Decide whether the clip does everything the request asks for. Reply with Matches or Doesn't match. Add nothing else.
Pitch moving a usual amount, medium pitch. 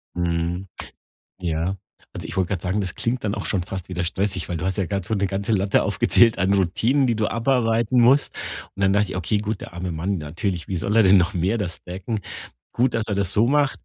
Doesn't match